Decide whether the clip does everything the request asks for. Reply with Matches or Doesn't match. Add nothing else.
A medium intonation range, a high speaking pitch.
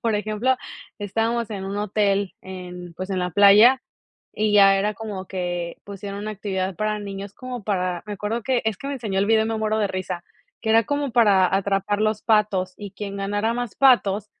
Doesn't match